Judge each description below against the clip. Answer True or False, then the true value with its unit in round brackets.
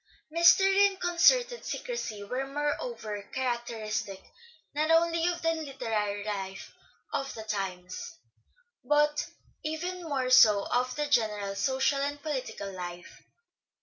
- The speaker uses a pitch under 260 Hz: False (270 Hz)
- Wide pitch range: True (7.6 semitones)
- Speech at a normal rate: False (115 wpm)